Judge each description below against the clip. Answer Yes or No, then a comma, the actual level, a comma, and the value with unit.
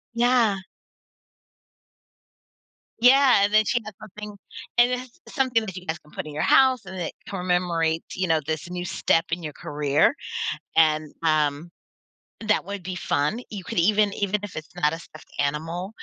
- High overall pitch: No, medium, 180 Hz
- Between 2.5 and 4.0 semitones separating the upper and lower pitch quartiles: No, average, 5.2 semitones